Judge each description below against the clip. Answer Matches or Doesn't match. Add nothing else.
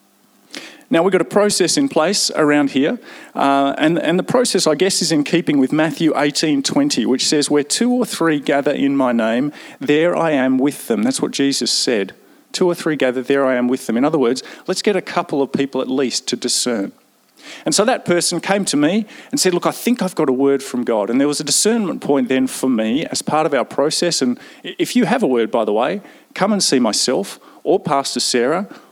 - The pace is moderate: Doesn't match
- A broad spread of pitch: Matches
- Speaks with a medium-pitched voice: Matches